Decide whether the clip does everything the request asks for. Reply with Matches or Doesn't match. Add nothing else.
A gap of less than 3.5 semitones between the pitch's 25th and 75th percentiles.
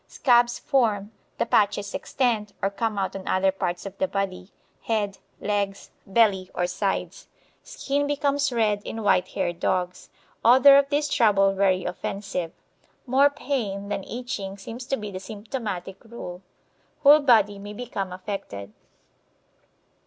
Doesn't match